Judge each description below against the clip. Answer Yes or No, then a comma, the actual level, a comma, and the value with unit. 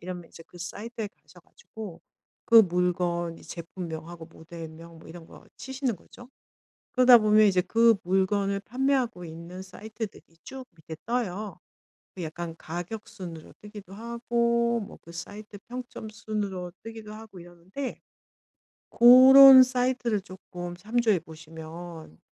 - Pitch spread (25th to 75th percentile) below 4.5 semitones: No, average, 5.1 semitones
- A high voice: Yes, high, 200 Hz